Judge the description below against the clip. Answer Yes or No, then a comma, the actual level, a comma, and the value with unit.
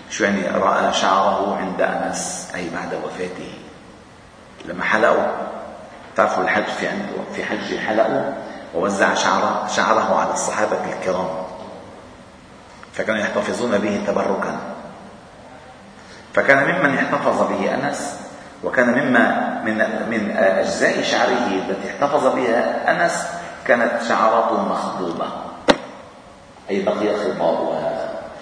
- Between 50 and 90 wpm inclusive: No, average, 105 wpm